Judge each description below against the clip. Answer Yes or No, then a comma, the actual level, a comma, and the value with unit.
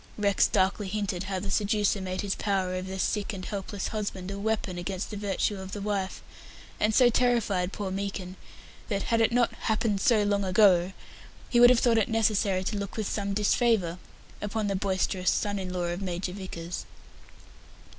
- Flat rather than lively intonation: Yes, narrow, 2.1 semitones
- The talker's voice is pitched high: Yes, high, 200 Hz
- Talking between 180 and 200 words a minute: Yes, average, 185 wpm